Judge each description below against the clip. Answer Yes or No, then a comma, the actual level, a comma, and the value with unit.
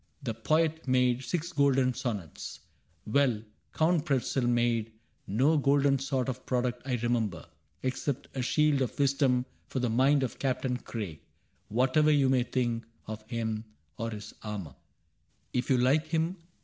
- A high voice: No, low, 130 Hz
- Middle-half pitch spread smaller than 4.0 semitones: Yes, average, 3.1 semitones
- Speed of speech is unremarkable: Yes, average, 155 wpm